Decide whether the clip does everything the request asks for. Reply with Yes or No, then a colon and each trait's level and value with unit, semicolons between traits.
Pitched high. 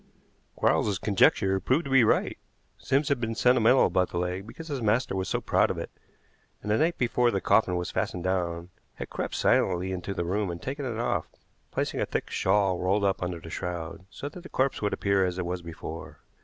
No: low, 100 Hz